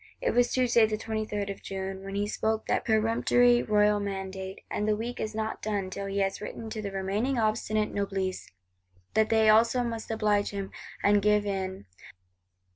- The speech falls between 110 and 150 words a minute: No, average, 180 wpm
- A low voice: No, high, 210 Hz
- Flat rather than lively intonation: Yes, narrow, 2.0 semitones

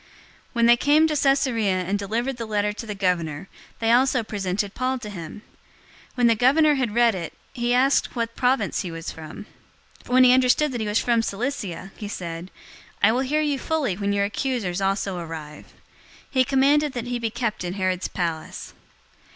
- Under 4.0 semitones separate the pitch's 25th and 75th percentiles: No, average, 5.0 semitones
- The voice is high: Yes, high, 225 Hz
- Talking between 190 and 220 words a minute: Yes, average, 195 wpm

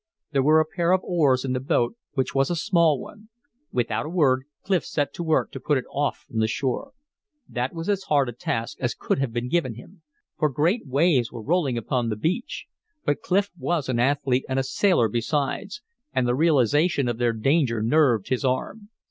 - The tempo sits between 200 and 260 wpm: Yes, fast, 205 wpm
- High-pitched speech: No, medium, 140 Hz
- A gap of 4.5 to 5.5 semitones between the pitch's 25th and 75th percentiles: Yes, average, 5.2 semitones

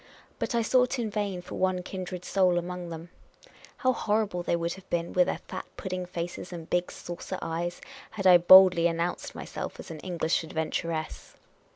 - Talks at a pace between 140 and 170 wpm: No, average, 180 wpm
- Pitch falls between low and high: Yes, medium, 180 Hz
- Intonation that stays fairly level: Yes, narrow, 1.9 semitones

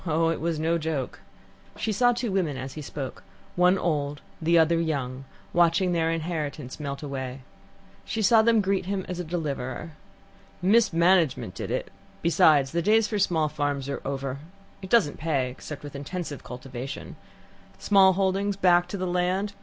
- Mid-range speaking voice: Yes, medium, 165 Hz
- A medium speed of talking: Yes, average, 170 wpm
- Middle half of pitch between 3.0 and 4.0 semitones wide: No, average, 4.7 semitones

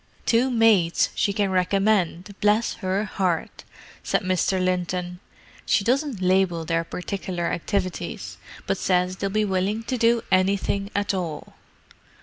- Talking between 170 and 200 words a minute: No, slow, 135 wpm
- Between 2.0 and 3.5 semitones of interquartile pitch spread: Yes, narrow, 2.6 semitones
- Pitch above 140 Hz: Yes, high, 190 Hz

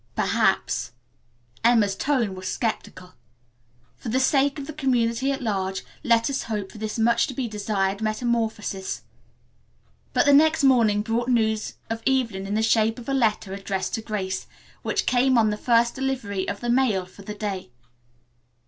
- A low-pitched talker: No, high, 225 Hz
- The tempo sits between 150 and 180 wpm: Yes, average, 165 wpm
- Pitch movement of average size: Yes, average, 3.8 semitones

